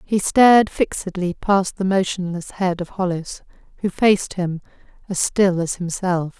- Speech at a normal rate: Yes, average, 150 wpm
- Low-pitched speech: No, medium, 185 Hz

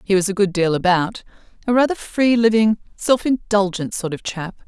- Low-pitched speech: No, high, 205 Hz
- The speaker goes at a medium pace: Yes, average, 180 wpm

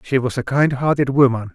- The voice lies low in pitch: Yes, low, 130 Hz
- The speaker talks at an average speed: No, fast, 235 wpm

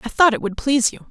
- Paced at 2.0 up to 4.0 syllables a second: No, 7.1 syllables/s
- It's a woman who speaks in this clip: Yes, female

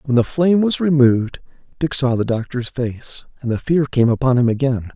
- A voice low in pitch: Yes, low, 130 Hz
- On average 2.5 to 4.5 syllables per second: No, 5.4 syllables/s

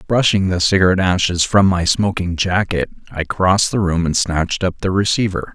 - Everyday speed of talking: Yes, average, 185 wpm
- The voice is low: Yes, very low, 90 Hz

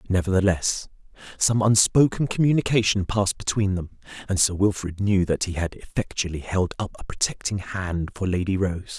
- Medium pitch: No, very low, 95 Hz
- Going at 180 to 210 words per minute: No, average, 155 wpm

